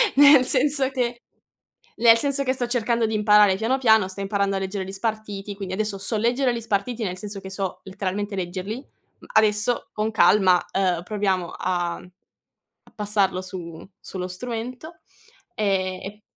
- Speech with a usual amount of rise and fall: Yes, average, 3.5 semitones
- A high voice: Yes, high, 210 Hz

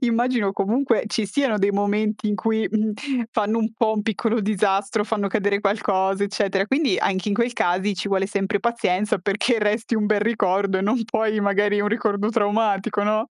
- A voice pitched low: No, high, 210 Hz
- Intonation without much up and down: Yes, narrow, 1.9 semitones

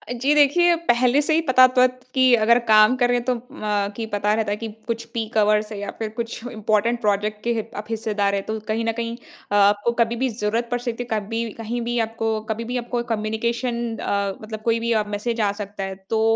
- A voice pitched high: Yes, high, 225 Hz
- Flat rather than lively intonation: Yes, narrow, 2.0 semitones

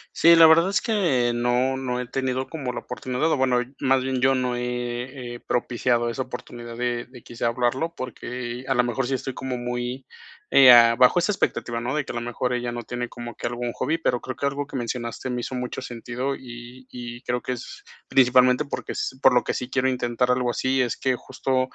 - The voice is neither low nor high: No, low, 125 Hz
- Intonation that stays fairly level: Yes, narrow, 1.4 semitones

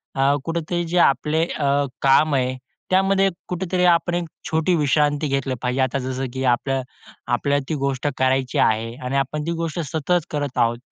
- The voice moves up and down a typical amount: Yes, average, 3.7 semitones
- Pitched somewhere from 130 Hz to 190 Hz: Yes, medium, 140 Hz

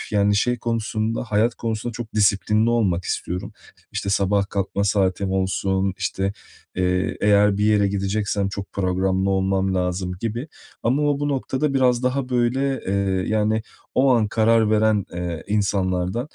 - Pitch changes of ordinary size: Yes, average, 3.1 semitones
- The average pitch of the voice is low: Yes, low, 105 Hz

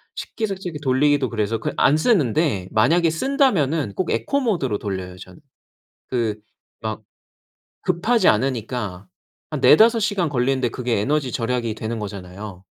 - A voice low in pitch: Yes, low, 130 Hz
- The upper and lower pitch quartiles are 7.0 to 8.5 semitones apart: Yes, wide, 7.8 semitones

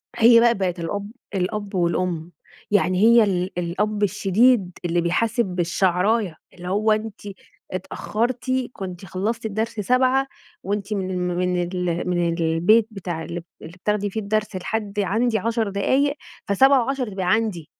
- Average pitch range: Yes, average, 3.6 semitones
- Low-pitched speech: No, high, 200 Hz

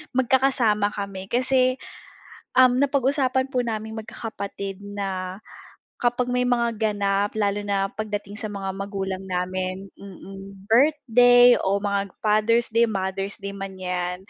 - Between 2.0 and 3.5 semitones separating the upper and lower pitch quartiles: No, average, 3.9 semitones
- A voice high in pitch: Yes, high, 205 Hz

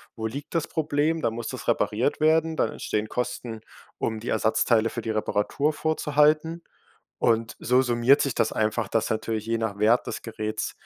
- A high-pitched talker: No, low, 120 Hz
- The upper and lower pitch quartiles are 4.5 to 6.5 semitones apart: Yes, average, 4.9 semitones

